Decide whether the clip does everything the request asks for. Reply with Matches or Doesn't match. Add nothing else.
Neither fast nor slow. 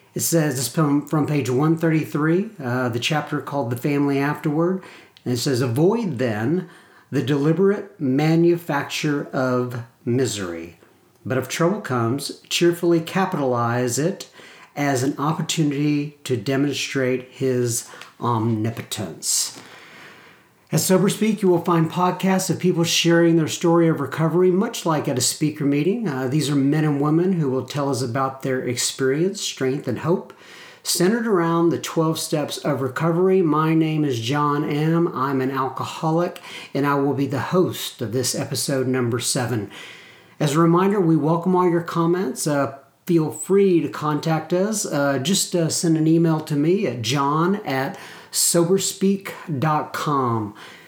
Matches